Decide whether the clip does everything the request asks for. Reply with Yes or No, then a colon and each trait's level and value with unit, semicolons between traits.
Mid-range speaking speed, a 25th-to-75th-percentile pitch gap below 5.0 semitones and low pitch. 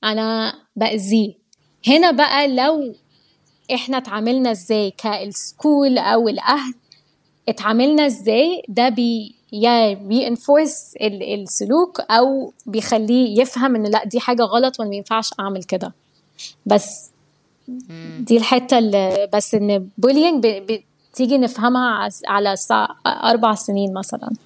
No: average, 105 wpm; average, 3.6 semitones; high, 225 Hz